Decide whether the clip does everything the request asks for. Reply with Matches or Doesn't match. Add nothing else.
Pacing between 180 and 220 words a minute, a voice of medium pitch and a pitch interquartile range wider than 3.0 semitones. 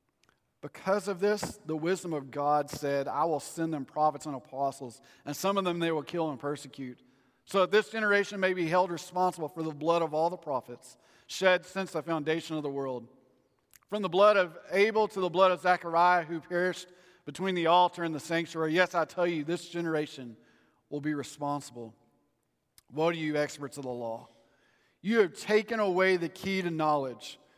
Matches